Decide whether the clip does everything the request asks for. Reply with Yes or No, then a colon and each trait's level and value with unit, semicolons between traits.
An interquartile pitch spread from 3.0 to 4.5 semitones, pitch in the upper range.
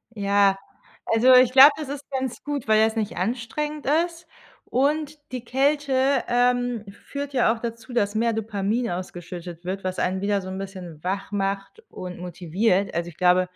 No: wide, 5.5 semitones; high, 220 Hz